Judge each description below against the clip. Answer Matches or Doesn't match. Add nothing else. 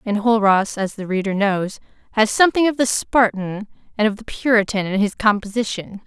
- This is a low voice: Doesn't match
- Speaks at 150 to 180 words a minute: Matches